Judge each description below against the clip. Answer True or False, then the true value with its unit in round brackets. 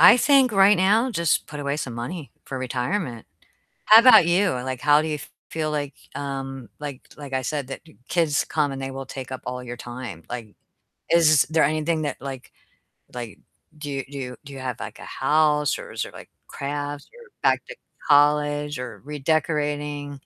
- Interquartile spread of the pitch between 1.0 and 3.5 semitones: True (3.0 semitones)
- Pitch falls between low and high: True (145 Hz)